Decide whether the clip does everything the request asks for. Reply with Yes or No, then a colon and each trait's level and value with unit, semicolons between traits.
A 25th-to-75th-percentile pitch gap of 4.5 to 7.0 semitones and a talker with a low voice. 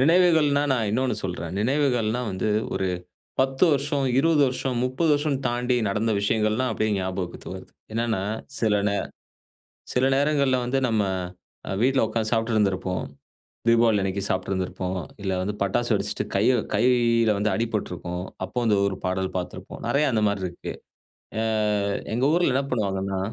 Yes: average, 5.1 semitones; low, 115 Hz